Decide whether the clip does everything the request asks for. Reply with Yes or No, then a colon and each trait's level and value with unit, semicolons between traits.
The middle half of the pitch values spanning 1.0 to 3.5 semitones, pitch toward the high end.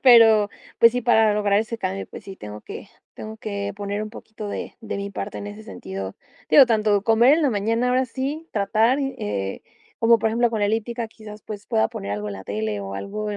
Yes: narrow, 2.5 semitones; high, 215 Hz